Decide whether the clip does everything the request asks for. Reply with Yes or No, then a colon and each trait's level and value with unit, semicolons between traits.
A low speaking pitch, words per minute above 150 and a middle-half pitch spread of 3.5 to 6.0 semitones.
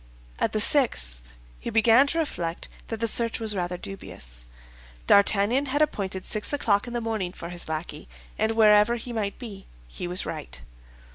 No: high, 210 Hz; average, 170 wpm; average, 4.7 semitones